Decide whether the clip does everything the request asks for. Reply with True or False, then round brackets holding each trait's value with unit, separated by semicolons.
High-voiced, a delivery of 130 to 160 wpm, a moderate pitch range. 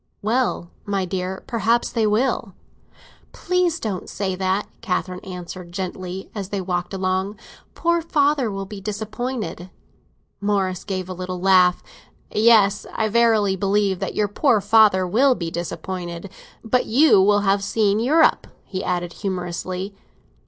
True (195 Hz; 140 wpm; 3.1 semitones)